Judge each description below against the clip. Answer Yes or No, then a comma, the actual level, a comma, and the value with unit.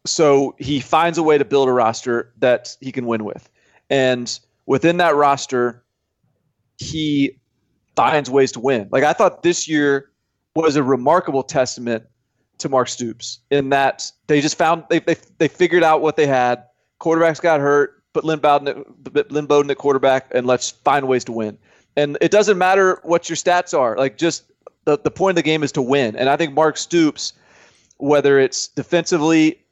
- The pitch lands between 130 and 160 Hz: Yes, medium, 140 Hz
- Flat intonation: No, average, 3.8 semitones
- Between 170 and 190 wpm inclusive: Yes, average, 180 wpm